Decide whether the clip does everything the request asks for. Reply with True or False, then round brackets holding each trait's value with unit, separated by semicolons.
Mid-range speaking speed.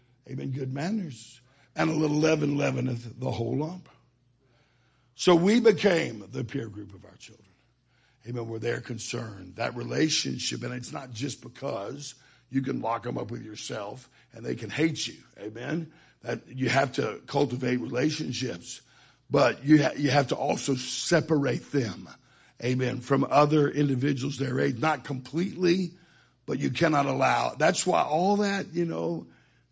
True (155 wpm)